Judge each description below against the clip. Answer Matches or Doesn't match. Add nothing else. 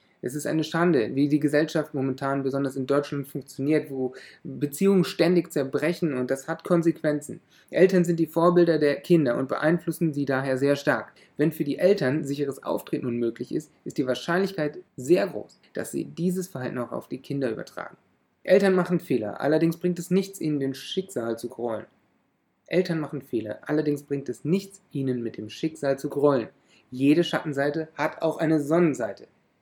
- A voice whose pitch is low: Doesn't match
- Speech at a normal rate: Matches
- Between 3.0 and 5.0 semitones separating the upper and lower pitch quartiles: Matches